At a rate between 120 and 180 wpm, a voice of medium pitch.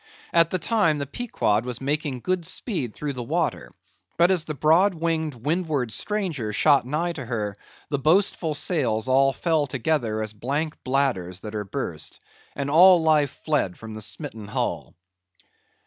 Yes: average, 165 wpm; medium, 145 Hz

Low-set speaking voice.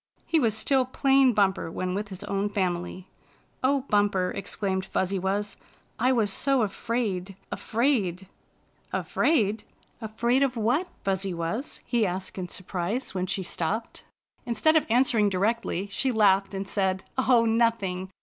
No: high, 205 Hz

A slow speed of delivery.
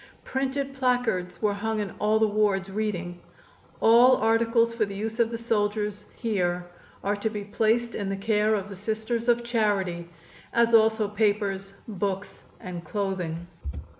No: average, 155 wpm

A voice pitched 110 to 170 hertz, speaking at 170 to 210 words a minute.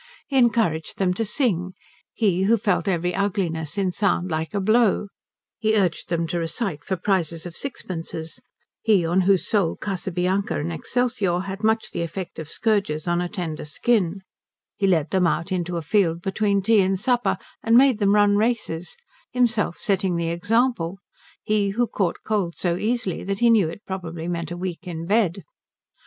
No: high, 190 Hz; average, 175 wpm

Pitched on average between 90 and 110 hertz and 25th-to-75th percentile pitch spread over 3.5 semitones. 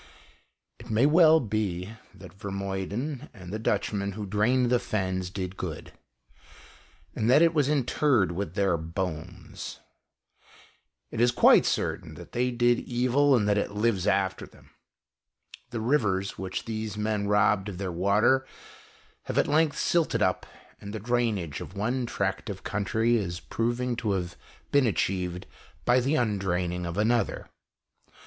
Yes: low, 105 Hz; average, 4.3 semitones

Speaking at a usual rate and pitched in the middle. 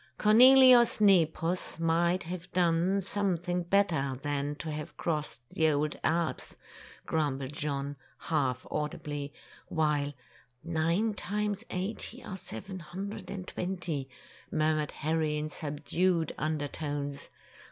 No: slow, 115 wpm; medium, 160 Hz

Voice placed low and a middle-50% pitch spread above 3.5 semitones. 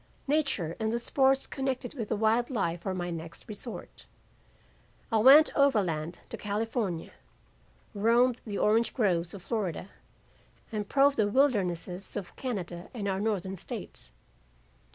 No: high, 215 Hz; average, 5.1 semitones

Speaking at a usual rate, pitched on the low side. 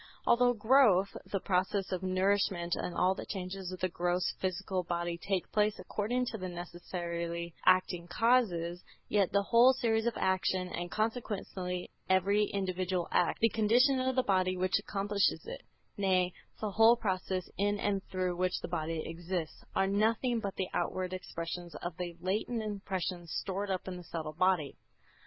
No: average, 165 wpm; medium, 185 Hz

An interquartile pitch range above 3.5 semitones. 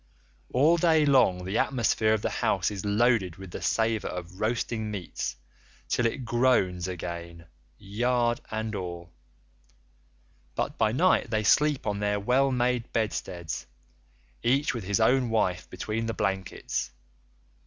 Yes: average, 4.4 semitones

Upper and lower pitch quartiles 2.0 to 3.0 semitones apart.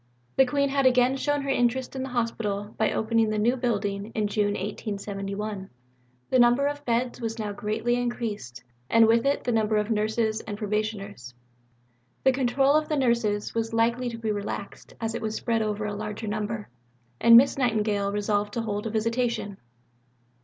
Yes: average, 2.7 semitones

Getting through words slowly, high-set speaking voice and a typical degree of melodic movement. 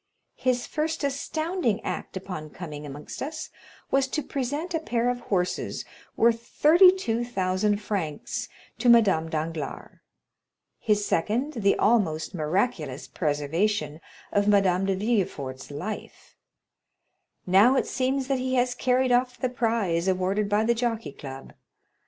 No: slow, 130 wpm; high, 215 Hz; wide, 6.0 semitones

